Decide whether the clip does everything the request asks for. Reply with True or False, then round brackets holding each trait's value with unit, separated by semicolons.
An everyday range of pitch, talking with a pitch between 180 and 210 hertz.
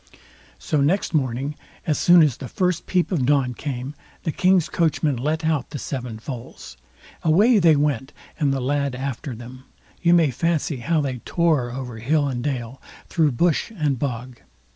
False (4.1 semitones; 145 Hz)